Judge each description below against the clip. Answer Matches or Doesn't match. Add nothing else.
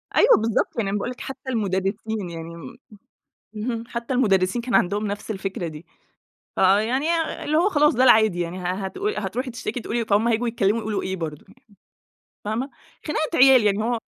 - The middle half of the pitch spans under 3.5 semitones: Doesn't match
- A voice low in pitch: Doesn't match